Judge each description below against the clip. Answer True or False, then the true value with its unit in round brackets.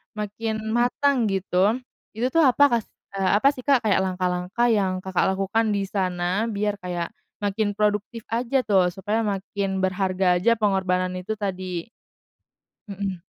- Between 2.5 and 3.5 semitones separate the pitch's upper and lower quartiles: True (3.1 semitones)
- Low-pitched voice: False (200 Hz)